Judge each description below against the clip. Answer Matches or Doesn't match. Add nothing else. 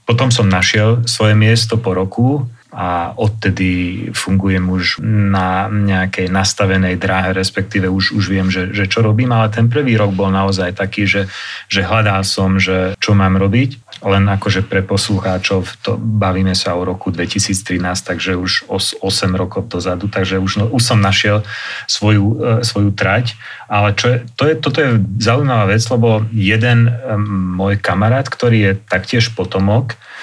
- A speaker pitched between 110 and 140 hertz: Doesn't match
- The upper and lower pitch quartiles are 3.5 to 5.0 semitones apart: Doesn't match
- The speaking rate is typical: Matches